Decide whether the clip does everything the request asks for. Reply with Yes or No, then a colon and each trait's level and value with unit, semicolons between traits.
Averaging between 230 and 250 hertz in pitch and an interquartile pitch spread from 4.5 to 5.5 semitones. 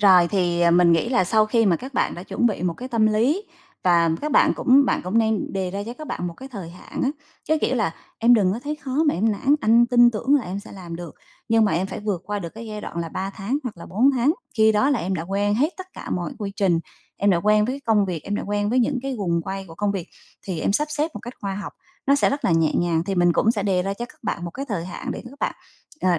No: high, 205 Hz; average, 5.1 semitones